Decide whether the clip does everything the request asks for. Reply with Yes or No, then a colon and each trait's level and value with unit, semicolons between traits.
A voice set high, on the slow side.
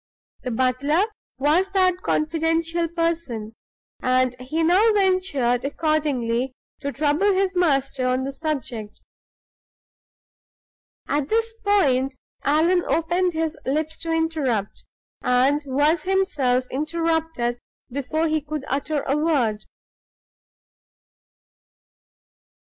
Yes: very high, 305 Hz; slow, 100 wpm